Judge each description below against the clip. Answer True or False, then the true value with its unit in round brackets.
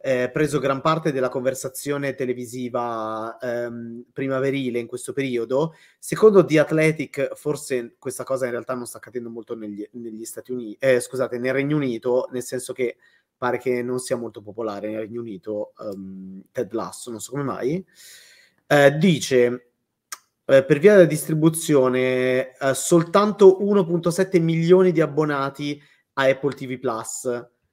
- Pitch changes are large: False (3.9 semitones)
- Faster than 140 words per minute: True (150 wpm)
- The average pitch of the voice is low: True (130 Hz)